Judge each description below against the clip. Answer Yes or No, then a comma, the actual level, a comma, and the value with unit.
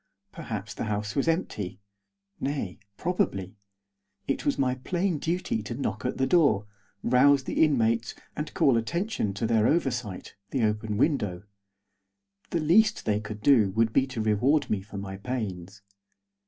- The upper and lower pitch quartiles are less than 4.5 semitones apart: No, wide, 5.6 semitones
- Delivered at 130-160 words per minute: Yes, average, 155 wpm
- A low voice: Yes, low, 115 Hz